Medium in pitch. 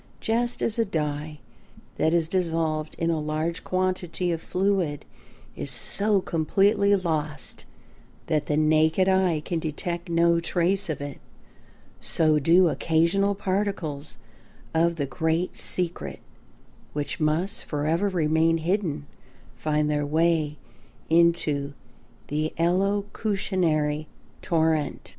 Yes: medium, 165 Hz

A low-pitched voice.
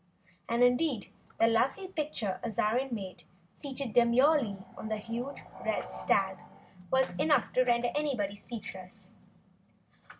No: high, 235 Hz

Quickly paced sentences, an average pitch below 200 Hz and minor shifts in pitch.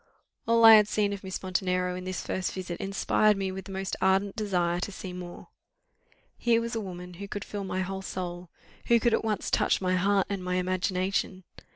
Yes: fast, 210 wpm; high, 190 Hz; narrow, 1.9 semitones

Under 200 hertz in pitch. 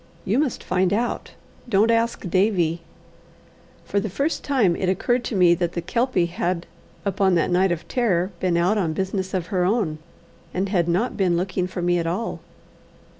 Yes: medium, 185 Hz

